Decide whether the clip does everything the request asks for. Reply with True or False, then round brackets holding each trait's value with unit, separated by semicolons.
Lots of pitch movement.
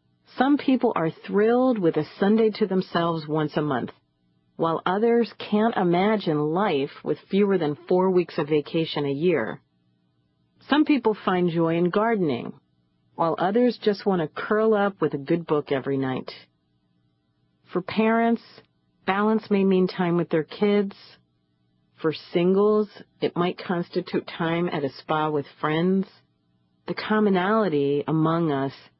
True (6.7 semitones)